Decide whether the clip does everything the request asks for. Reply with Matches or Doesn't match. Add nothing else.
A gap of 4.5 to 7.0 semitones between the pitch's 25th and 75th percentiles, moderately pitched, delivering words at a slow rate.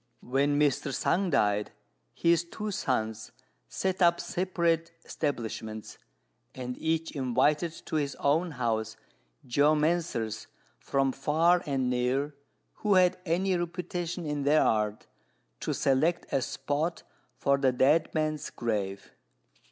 Matches